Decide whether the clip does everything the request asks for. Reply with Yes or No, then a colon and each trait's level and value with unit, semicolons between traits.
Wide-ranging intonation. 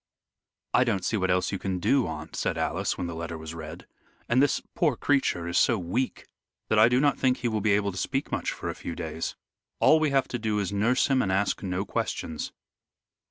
Yes: wide, 6.4 semitones